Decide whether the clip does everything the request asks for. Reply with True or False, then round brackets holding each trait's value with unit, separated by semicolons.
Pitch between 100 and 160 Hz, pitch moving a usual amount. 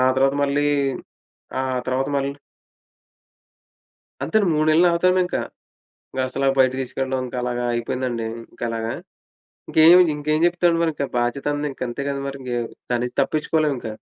True (135 Hz; 3.7 semitones)